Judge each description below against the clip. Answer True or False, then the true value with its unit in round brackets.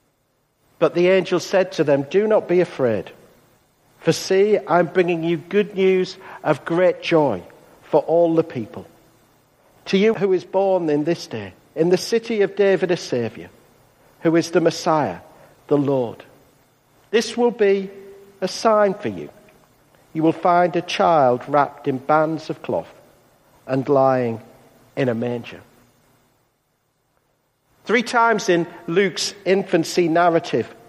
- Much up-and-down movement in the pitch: True (6.0 semitones)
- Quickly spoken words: False (140 wpm)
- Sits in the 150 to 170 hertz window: True (165 Hz)